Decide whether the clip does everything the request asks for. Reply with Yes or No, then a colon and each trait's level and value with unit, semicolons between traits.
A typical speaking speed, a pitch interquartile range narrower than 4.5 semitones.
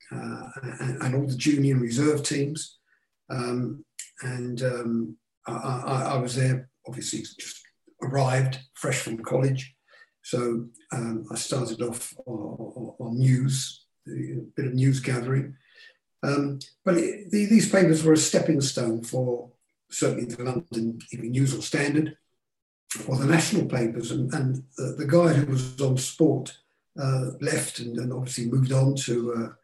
Yes: average, 155 wpm; average, 2.8 semitones